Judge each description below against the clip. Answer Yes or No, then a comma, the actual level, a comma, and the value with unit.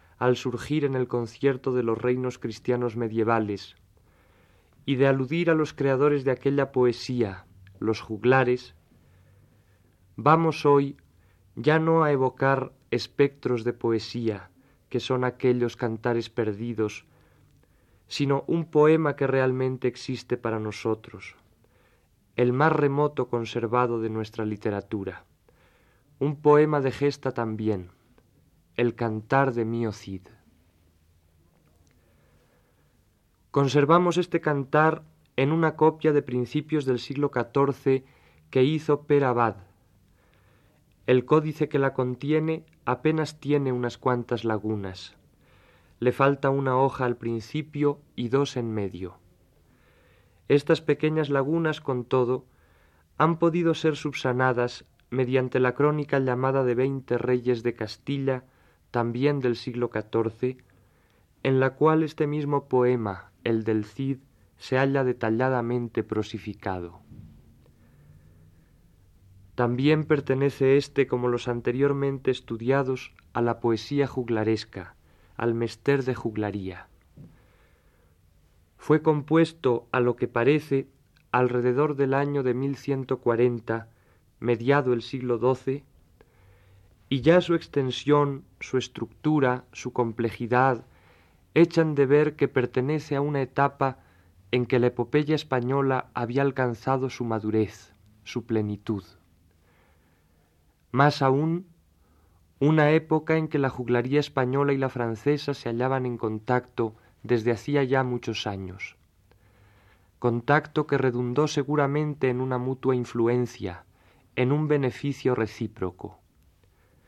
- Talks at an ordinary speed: No, slow, 110 wpm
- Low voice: Yes, low, 125 Hz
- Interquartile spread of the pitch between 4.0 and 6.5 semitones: Yes, average, 4.6 semitones